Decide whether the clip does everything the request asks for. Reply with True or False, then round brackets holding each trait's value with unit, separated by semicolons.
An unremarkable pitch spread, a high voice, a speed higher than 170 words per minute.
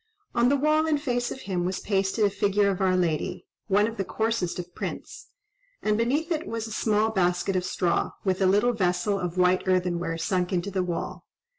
True (4.0 semitones; 195 Hz; 195 wpm)